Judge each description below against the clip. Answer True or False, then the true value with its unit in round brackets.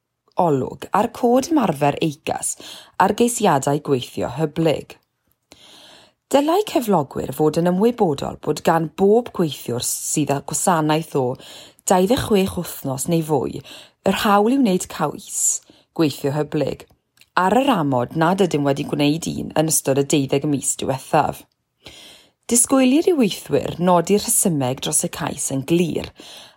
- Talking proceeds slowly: True (130 wpm)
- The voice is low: False (165 Hz)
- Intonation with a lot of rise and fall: True (6.0 semitones)